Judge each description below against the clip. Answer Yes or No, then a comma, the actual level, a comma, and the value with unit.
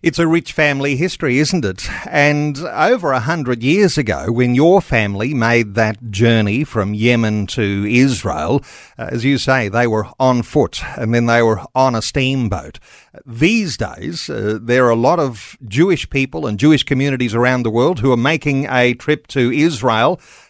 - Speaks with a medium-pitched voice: No, low, 125 Hz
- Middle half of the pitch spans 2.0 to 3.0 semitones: No, average, 4.2 semitones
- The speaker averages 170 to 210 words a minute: Yes, average, 175 wpm